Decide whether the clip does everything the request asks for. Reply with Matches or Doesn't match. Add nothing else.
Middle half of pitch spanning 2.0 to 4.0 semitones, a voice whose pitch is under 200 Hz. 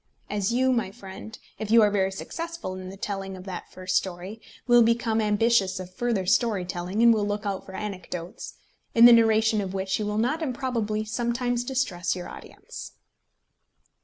Doesn't match